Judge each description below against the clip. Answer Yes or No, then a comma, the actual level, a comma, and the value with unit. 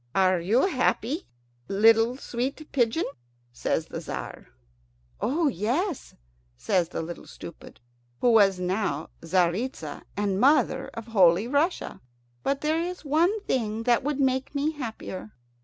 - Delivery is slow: Yes, slow, 130 wpm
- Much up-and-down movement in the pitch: Yes, wide, 6.8 semitones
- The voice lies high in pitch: Yes, high, 235 Hz